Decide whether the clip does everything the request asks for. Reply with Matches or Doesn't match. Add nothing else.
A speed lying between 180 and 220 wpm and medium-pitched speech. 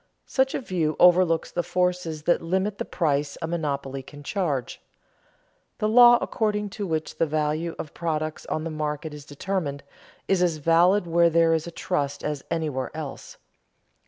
Doesn't match